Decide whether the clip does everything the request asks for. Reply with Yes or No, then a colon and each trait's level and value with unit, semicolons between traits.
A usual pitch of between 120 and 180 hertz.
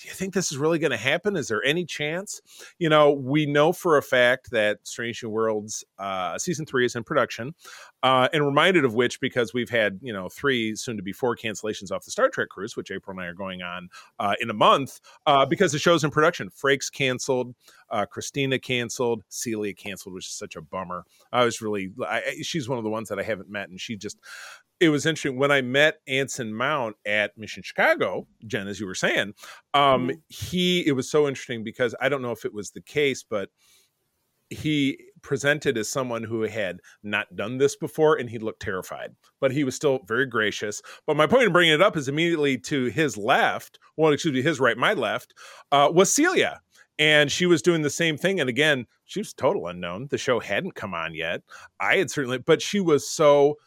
Yes: low, 135 Hz